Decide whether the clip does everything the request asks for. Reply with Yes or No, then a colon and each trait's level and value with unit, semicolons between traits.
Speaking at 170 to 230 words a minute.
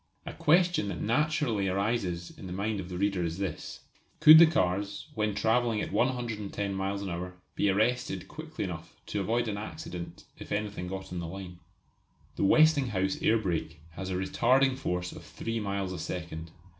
Yes: average, 180 wpm